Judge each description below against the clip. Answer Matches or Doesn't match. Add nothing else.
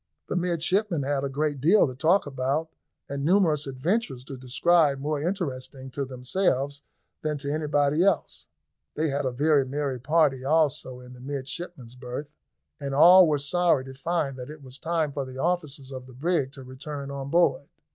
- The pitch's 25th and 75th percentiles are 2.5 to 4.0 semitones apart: Matches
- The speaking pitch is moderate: Matches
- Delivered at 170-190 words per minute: Matches